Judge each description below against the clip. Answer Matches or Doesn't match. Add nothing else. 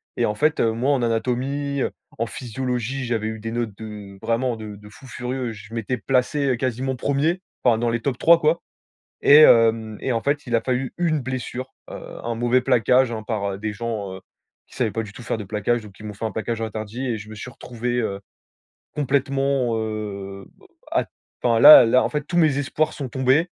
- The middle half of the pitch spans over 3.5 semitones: Doesn't match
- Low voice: Matches